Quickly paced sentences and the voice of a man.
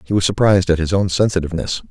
Yes: fast, 220 wpm; male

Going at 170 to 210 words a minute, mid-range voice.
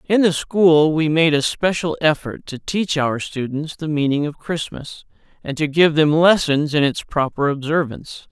Yes: average, 180 wpm; medium, 155 Hz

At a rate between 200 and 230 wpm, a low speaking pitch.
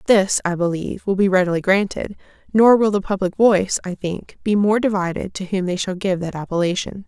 No: fast, 205 wpm; high, 190 Hz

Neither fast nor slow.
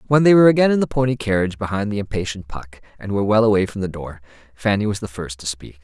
No: fast, 255 wpm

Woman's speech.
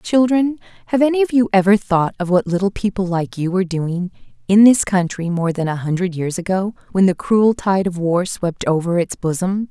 Yes: female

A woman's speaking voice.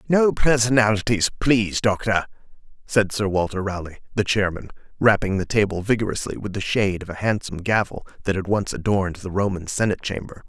No: male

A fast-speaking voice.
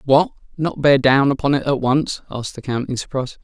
Yes: fast, 225 wpm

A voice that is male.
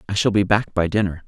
Yes: male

